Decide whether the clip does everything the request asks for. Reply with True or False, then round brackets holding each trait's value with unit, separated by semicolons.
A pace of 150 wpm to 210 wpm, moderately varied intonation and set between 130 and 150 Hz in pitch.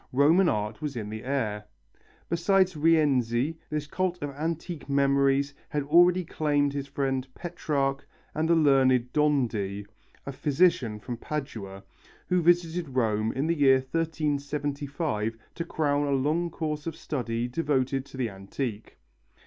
False (140 wpm; 3.9 semitones; 140 Hz)